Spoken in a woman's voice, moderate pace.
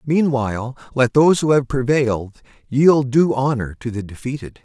No: male; average, 155 wpm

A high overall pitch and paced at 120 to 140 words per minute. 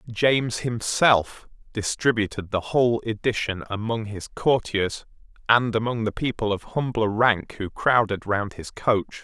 No: low, 110 Hz; slow, 135 wpm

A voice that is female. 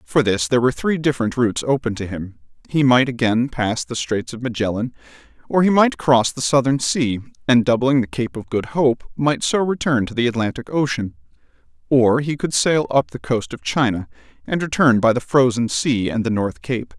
No: male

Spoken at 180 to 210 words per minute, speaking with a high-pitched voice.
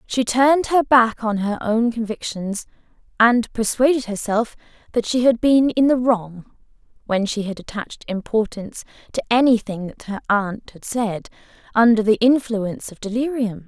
No: average, 155 wpm; high, 225 Hz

